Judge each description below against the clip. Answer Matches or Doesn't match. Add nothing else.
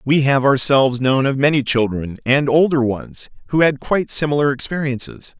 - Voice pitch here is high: Doesn't match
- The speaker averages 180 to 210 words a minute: Doesn't match